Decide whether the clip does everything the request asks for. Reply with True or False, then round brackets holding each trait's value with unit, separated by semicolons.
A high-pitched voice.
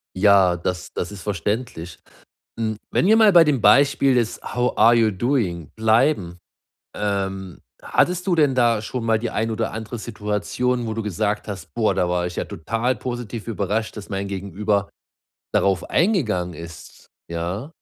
False (110 Hz)